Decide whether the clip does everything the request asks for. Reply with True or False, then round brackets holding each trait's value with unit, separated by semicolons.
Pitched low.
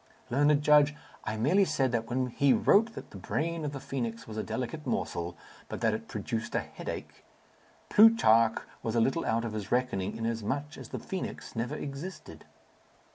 True (130 Hz)